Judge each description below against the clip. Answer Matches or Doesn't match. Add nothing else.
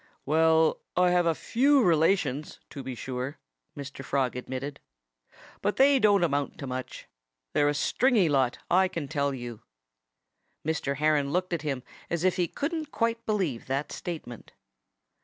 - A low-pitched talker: Doesn't match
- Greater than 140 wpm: Matches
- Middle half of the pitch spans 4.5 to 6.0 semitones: Matches